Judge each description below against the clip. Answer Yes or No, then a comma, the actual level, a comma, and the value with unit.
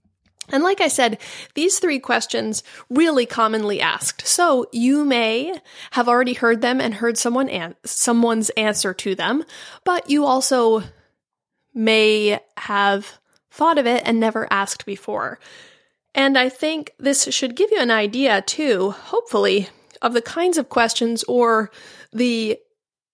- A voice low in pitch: No, high, 245 Hz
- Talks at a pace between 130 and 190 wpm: Yes, average, 145 wpm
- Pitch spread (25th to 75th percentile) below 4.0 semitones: No, average, 4.7 semitones